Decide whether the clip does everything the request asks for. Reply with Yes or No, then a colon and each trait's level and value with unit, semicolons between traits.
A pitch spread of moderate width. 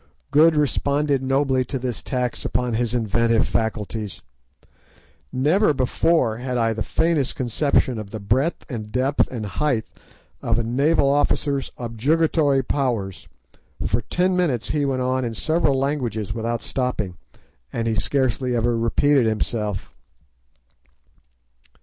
Yes: average, 3.8 semitones